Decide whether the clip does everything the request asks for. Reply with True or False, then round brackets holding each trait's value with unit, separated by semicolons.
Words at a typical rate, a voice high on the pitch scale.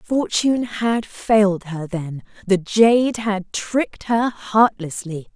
False (125 wpm; 205 Hz)